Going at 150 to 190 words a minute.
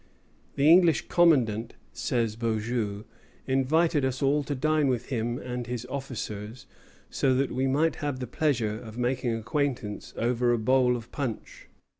Yes: average, 155 wpm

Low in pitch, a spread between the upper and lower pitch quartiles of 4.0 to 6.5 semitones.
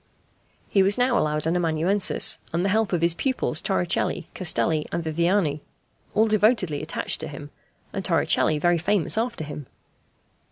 No: medium, 175 Hz; average, 4.6 semitones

